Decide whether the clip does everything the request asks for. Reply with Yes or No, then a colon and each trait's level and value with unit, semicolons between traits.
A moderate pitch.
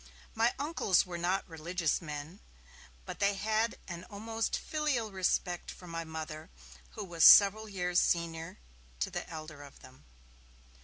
Yes: medium, 180 Hz